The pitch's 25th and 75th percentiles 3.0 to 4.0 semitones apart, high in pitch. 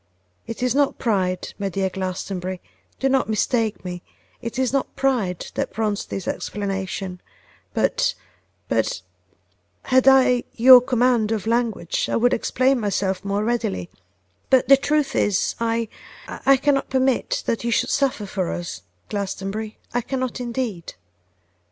No: average, 4.8 semitones; high, 230 Hz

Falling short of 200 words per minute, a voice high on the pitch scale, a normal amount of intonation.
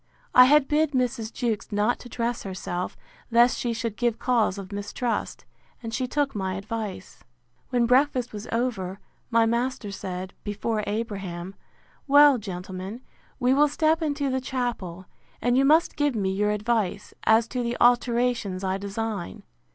Yes: average, 155 wpm; high, 230 Hz; average, 3.9 semitones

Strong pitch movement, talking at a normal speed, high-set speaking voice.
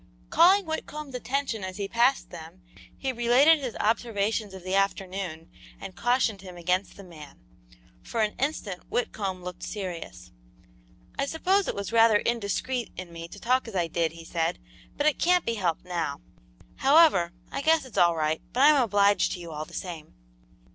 Yes: wide, 6.5 semitones; average, 175 wpm; high, 200 Hz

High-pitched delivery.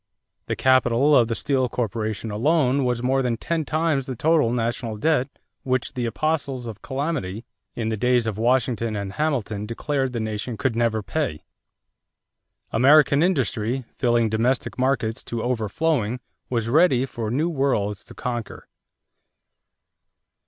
No: low, 125 Hz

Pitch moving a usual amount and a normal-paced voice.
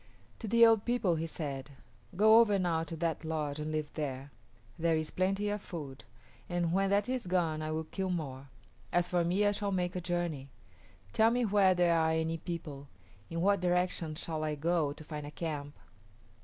Yes: average, 3.6 semitones; average, 195 wpm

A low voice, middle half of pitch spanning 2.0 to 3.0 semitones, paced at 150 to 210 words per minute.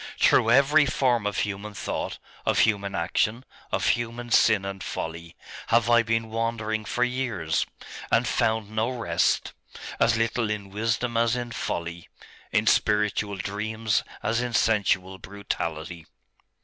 No: low, 110 Hz; average, 2.7 semitones; slow, 135 wpm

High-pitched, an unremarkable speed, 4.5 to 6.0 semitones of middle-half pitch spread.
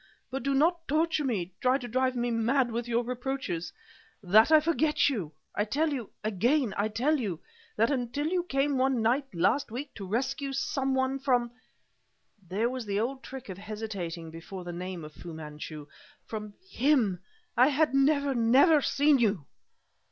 Yes: high, 245 Hz; average, 175 wpm; average, 5.1 semitones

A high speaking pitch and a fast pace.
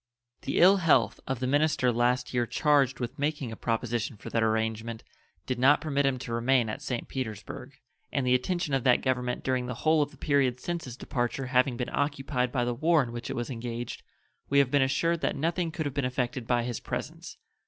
No: low, 130 Hz; fast, 215 wpm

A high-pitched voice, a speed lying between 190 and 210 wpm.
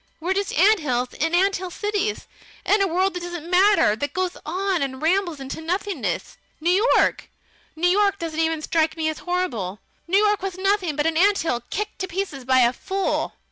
Yes: very high, 355 Hz; average, 195 wpm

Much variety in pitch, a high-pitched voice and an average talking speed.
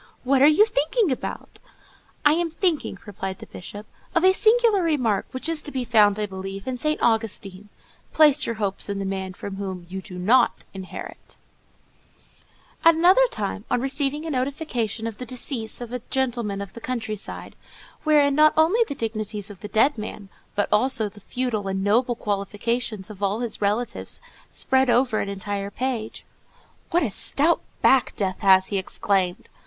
Yes: wide, 5.7 semitones; high, 230 Hz; average, 175 wpm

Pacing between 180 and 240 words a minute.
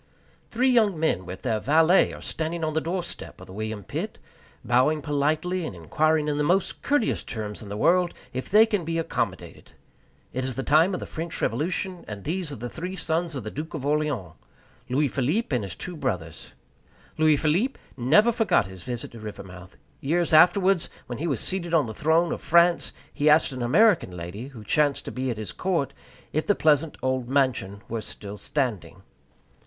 Yes: average, 190 wpm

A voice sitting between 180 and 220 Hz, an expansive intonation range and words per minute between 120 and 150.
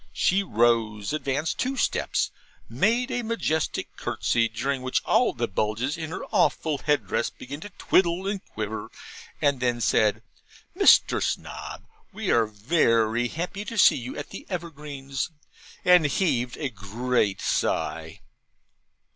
No: medium, 140 Hz; wide, 6.8 semitones; average, 140 wpm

